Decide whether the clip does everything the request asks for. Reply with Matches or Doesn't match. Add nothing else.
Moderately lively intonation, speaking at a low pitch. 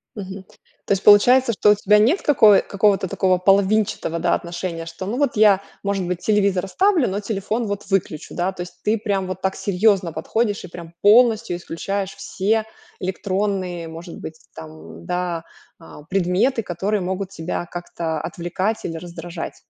Doesn't match